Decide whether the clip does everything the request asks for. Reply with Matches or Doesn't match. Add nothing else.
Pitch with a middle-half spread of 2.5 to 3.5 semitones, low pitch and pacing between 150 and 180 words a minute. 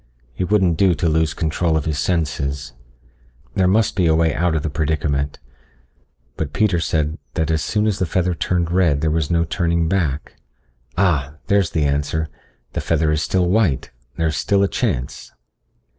Matches